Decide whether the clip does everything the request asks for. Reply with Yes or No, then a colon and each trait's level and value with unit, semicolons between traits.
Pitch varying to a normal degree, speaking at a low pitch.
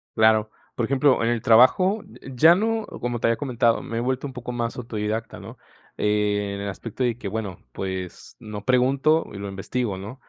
Yes: average, 3.5 semitones; low, 115 Hz